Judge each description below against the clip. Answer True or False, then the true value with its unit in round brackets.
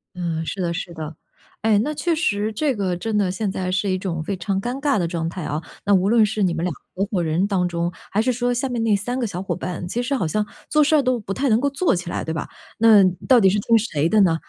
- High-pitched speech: True (200 Hz)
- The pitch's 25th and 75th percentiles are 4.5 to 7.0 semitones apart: True (4.8 semitones)